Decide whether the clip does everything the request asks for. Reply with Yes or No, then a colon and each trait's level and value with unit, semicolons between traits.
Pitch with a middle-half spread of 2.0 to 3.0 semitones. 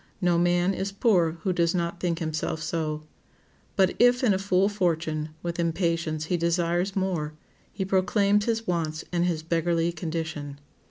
Yes: average, 2.7 semitones